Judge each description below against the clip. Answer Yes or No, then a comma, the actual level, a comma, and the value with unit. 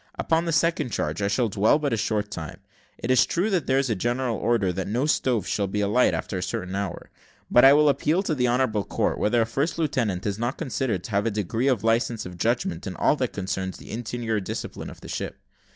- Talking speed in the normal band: No, fast, 240 wpm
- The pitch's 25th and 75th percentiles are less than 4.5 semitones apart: No, average, 4.8 semitones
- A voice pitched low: Yes, low, 115 Hz